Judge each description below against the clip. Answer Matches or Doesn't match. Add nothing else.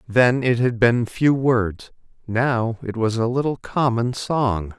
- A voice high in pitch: Doesn't match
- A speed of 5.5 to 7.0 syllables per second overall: Doesn't match